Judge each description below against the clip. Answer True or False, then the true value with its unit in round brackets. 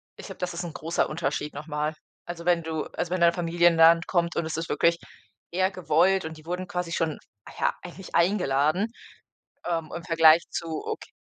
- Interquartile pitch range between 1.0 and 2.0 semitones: True (1.7 semitones)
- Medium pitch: True (170 Hz)